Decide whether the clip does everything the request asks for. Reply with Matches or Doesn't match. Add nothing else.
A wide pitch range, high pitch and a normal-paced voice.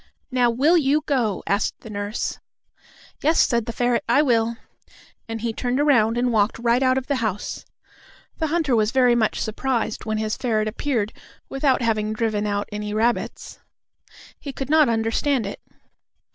Doesn't match